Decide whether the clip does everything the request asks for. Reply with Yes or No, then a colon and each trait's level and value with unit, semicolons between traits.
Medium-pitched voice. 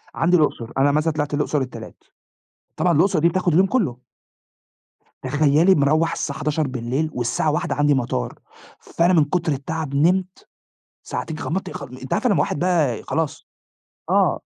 Yes: medium, 155 Hz